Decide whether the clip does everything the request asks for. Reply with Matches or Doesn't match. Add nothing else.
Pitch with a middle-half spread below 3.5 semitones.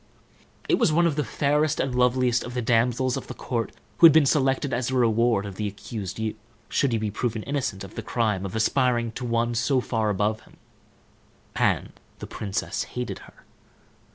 Matches